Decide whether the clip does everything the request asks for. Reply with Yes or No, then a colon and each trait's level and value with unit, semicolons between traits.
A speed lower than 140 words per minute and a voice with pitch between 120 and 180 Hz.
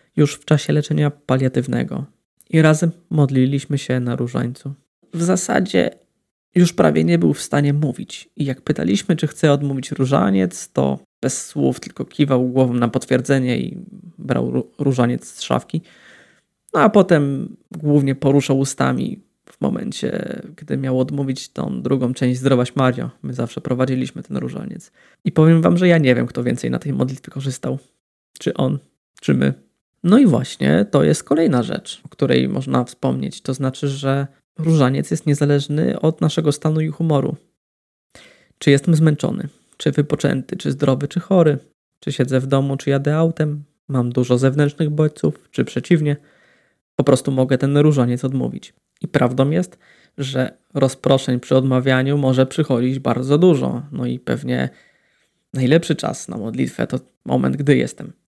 No: average, 155 wpm; medium, 140 Hz